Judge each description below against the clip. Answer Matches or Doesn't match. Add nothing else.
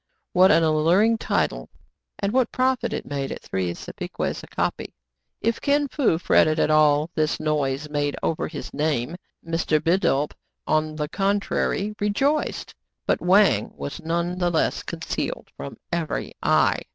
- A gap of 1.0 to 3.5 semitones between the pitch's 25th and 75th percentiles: Doesn't match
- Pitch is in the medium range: Matches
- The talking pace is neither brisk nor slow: Matches